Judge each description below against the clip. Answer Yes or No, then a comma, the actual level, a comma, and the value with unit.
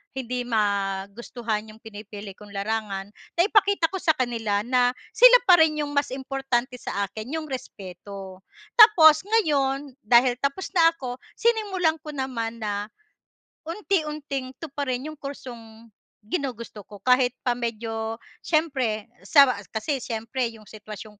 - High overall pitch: Yes, very high, 250 Hz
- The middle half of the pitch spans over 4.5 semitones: Yes, wide, 5.6 semitones